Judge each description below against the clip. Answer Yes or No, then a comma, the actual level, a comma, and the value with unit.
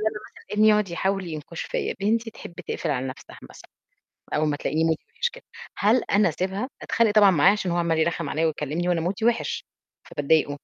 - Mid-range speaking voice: Yes, medium, 175 Hz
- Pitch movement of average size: Yes, average, 5.0 semitones